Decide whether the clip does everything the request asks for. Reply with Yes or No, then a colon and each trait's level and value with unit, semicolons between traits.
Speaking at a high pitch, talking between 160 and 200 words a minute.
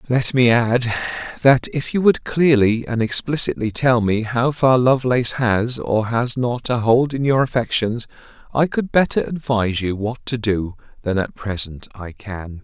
No: low, 120 Hz; average, 175 wpm